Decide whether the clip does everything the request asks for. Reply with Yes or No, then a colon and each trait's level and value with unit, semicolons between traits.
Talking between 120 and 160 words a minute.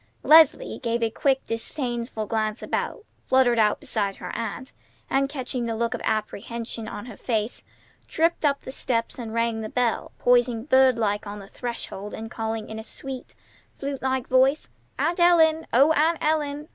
No: average, 170 wpm